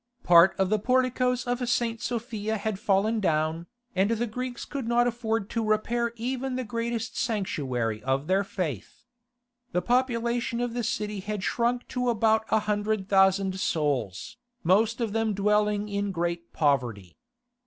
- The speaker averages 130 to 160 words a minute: Yes, average, 155 wpm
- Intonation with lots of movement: No, average, 3.9 semitones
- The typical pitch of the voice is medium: No, high, 215 Hz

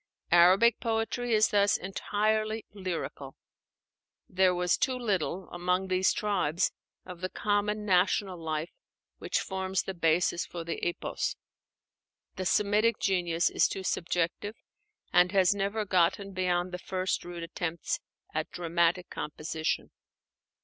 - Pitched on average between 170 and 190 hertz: Yes, medium, 185 Hz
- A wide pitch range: No, average, 2.8 semitones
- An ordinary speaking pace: No, slow, 125 wpm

